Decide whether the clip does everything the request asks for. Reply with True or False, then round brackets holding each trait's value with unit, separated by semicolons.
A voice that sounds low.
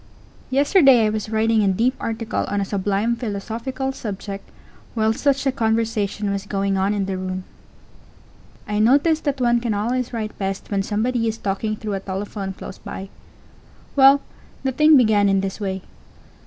False (215 Hz)